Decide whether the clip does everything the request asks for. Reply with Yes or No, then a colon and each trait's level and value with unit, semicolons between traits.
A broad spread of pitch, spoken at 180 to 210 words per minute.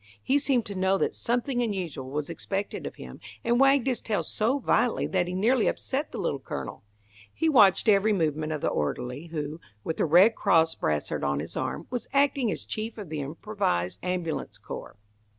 Yes: wide, 7.3 semitones; average, 190 wpm